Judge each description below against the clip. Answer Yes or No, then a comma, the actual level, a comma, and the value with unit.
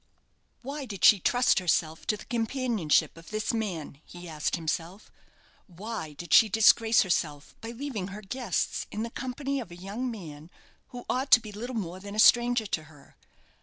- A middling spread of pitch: No, wide, 5.7 semitones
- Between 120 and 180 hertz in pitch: No, high, 210 Hz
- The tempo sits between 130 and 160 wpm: No, average, 180 wpm